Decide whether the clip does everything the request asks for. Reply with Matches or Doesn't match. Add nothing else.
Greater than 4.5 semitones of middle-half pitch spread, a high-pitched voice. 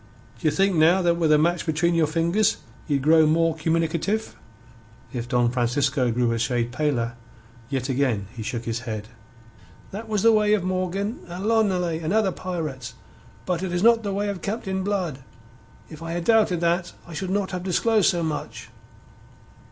Doesn't match